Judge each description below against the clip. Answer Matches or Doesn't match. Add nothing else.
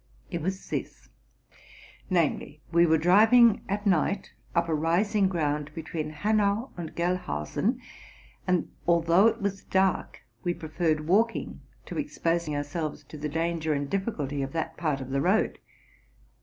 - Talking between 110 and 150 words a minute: Matches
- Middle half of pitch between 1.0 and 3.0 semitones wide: Doesn't match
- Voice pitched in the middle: Matches